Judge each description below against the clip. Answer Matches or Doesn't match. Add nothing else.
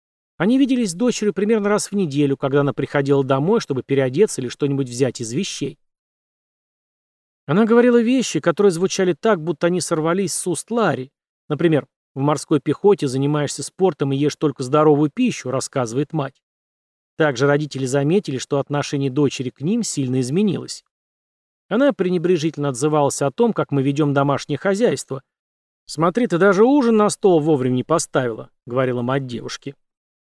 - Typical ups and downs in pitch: Doesn't match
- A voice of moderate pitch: Matches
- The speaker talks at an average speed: Matches